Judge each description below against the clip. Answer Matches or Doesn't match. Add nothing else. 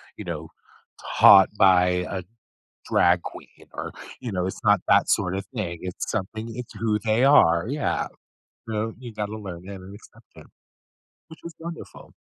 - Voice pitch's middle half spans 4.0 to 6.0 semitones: Doesn't match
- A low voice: Matches